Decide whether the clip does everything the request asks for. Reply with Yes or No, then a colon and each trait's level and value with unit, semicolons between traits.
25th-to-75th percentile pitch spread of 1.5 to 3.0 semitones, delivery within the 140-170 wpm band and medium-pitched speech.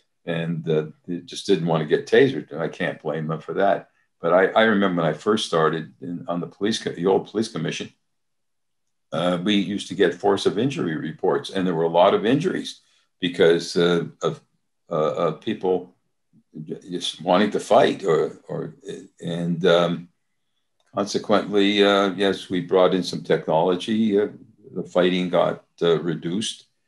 No: narrow, 2.6 semitones; average, 165 wpm; very low, 90 Hz